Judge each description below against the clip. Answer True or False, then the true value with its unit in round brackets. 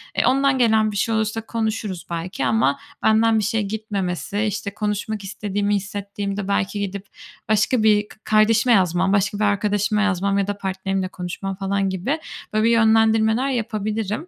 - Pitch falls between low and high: False (205 Hz)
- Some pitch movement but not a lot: False (2.0 semitones)